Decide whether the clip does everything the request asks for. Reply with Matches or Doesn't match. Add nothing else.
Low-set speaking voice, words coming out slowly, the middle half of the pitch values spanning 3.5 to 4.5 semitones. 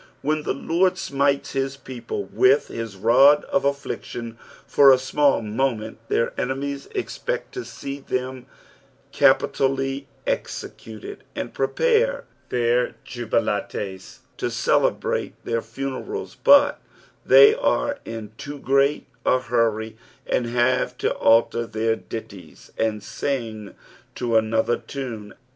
Matches